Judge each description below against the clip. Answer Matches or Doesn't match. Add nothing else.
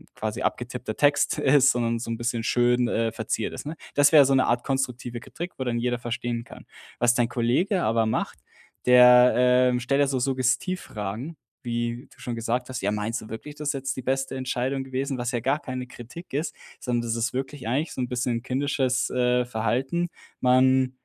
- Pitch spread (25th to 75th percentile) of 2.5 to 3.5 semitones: Doesn't match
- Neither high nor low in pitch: Doesn't match